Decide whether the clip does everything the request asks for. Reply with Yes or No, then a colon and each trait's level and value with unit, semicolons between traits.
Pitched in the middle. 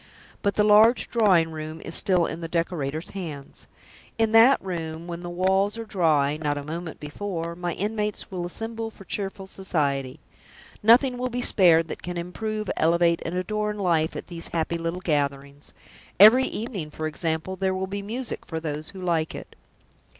Yes: medium, 175 Hz